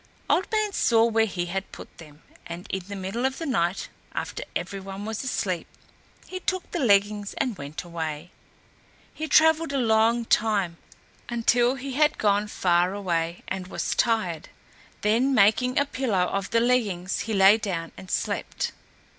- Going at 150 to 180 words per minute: Yes, average, 165 wpm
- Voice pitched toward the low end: No, high, 210 Hz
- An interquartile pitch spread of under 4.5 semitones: No, average, 5.1 semitones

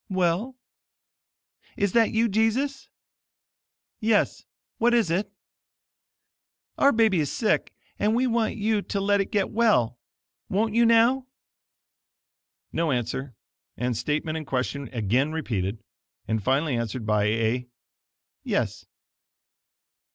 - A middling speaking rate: No, slow, 115 wpm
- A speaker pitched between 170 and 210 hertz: Yes, medium, 185 Hz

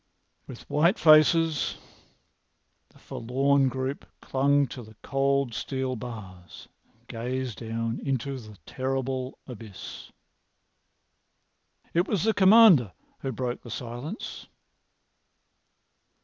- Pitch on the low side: Yes, low, 130 Hz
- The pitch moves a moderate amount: Yes, average, 3.1 semitones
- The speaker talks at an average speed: No, slow, 100 wpm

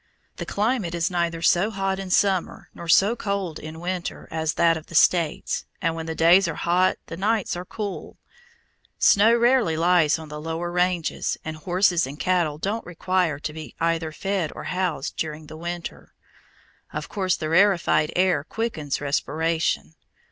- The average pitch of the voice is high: No, medium, 170 Hz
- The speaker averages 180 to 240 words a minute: No, average, 170 wpm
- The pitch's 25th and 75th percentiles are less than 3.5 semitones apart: Yes, average, 2.8 semitones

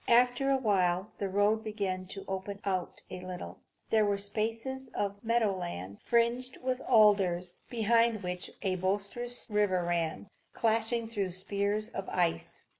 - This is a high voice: Yes, high, 205 Hz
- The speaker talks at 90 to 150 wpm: Yes, average, 145 wpm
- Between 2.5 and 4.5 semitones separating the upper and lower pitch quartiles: Yes, average, 3.7 semitones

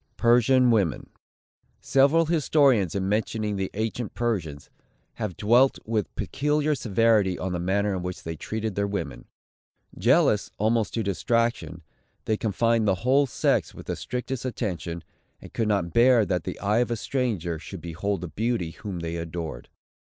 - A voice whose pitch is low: Yes, low, 105 Hz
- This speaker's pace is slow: No, average, 155 wpm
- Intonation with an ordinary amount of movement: Yes, average, 4.6 semitones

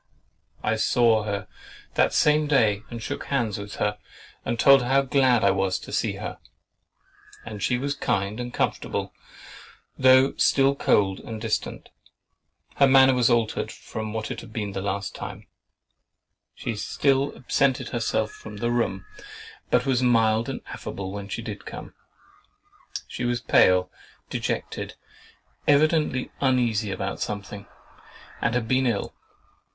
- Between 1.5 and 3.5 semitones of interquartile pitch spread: No, average, 4.0 semitones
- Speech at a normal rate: Yes, average, 145 wpm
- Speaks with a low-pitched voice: Yes, low, 115 Hz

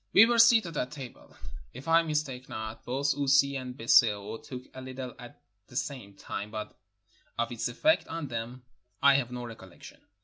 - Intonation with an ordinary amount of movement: Yes, average, 3.4 semitones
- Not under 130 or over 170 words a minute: No, average, 180 wpm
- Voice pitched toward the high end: No, low, 130 Hz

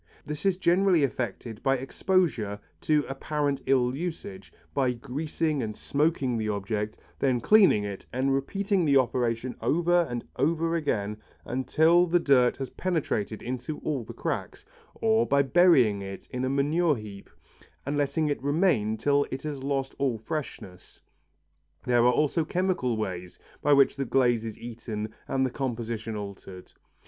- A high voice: No, low, 135 Hz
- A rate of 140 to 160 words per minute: Yes, average, 155 wpm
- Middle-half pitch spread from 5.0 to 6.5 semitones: Yes, average, 5.3 semitones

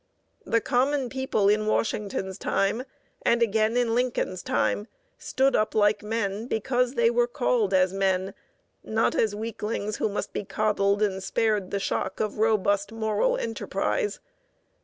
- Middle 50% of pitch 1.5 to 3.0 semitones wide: Yes, average, 2.7 semitones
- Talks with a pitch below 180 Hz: No, high, 215 Hz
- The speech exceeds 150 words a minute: No, average, 145 wpm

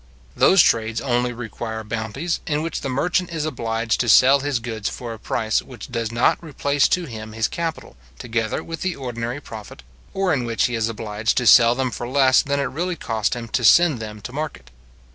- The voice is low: Yes, low, 120 Hz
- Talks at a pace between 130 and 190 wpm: No, fast, 205 wpm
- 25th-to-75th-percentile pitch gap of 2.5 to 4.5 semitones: Yes, average, 4.1 semitones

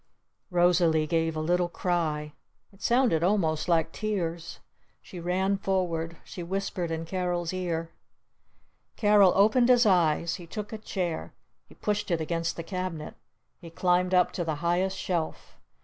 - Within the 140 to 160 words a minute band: Yes, average, 150 wpm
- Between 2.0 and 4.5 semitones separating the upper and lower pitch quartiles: Yes, narrow, 2.6 semitones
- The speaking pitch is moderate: Yes, medium, 175 Hz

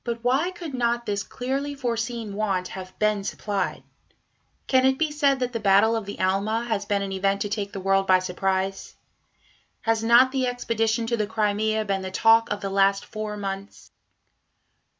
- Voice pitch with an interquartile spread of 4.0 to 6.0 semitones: No, average, 3.3 semitones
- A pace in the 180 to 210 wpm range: Yes, average, 185 wpm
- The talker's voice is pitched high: Yes, high, 215 Hz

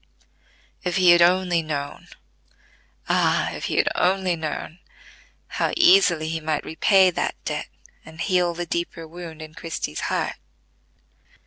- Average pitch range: No, narrow, 2.3 semitones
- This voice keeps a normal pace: No, slow, 125 wpm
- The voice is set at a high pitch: No, medium, 170 Hz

